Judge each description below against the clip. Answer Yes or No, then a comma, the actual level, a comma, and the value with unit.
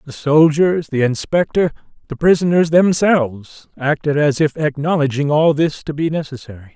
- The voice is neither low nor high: Yes, medium, 150 Hz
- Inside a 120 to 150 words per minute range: Yes, average, 140 wpm